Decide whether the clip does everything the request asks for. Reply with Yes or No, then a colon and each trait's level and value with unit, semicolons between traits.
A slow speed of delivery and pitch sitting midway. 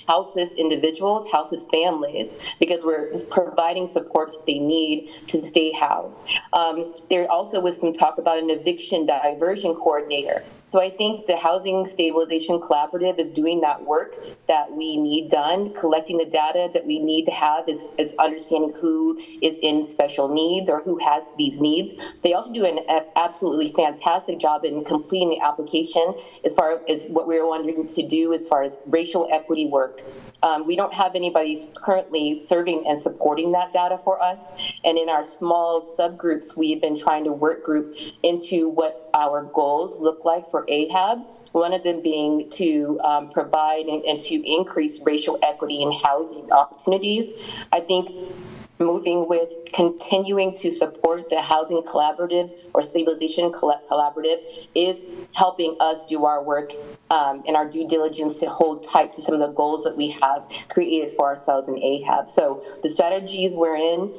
No: average, 165 wpm; medium, 165 Hz